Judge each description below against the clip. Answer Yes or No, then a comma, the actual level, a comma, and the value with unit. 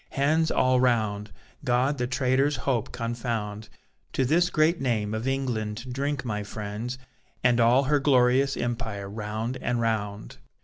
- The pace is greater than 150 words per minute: No, average, 140 wpm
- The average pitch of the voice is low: Yes, low, 125 Hz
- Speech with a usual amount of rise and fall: Yes, average, 3.5 semitones